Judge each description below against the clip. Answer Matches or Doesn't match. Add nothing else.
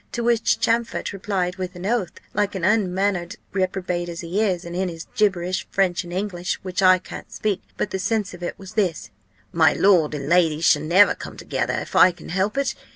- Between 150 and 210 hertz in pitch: Matches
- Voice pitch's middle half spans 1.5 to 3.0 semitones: Matches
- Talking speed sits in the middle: Doesn't match